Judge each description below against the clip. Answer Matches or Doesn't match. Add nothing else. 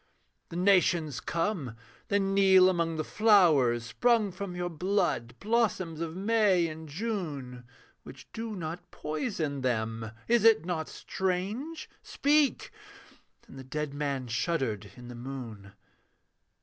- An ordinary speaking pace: Doesn't match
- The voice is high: Doesn't match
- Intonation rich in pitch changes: Matches